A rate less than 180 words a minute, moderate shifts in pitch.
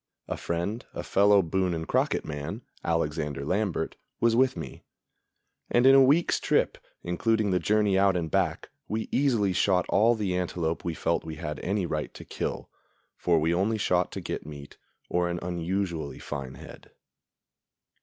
Yes: average, 165 wpm; average, 4.2 semitones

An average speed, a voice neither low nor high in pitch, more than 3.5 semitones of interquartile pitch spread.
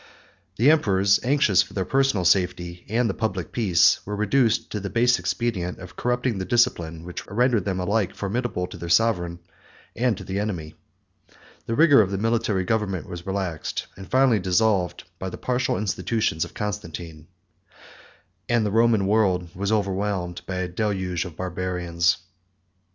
No: average, 160 wpm; low, 100 Hz; average, 4.0 semitones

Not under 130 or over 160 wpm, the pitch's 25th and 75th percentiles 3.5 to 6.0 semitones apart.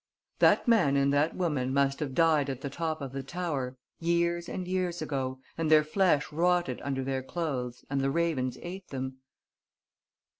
No: average, 175 wpm; average, 4.2 semitones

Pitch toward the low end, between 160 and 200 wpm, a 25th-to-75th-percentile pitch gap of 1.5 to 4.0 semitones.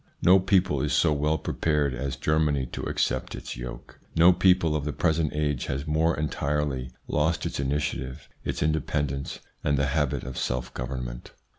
Yes: very low, 75 Hz; average, 165 wpm; average, 2.7 semitones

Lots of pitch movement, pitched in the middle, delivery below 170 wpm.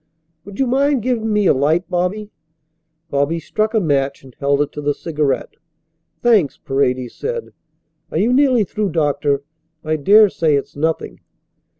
Yes: wide, 7.2 semitones; medium, 165 Hz; average, 155 wpm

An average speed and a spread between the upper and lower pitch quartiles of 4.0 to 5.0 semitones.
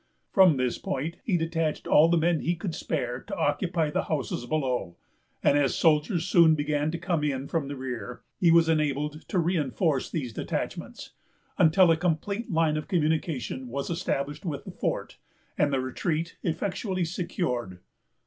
No: average, 170 wpm; average, 3.3 semitones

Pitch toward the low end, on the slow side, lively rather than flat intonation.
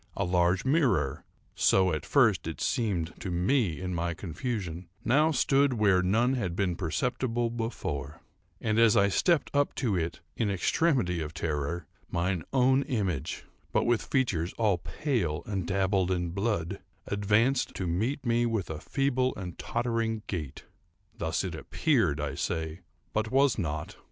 No: low, 100 Hz; average, 150 wpm; wide, 5.7 semitones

